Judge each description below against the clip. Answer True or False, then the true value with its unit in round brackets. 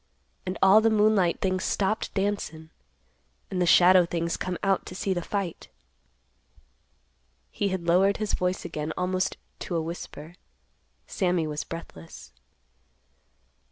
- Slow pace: True (130 wpm)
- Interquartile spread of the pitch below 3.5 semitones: True (2.5 semitones)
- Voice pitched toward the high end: False (180 Hz)